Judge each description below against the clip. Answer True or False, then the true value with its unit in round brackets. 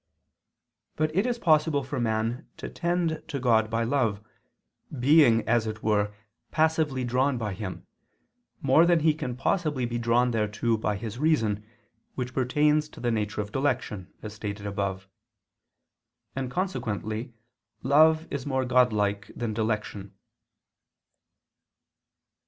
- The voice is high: False (120 Hz)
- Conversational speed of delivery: False (130 wpm)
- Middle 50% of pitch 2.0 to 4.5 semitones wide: False (5.4 semitones)